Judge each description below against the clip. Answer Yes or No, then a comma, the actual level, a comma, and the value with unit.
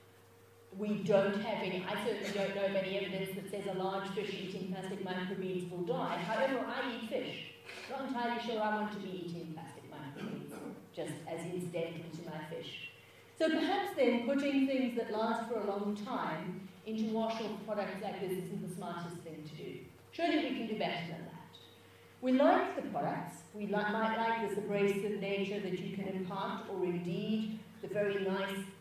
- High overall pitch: Yes, high, 200 Hz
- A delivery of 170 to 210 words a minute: Yes, average, 190 wpm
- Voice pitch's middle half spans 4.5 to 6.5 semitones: No, average, 3.2 semitones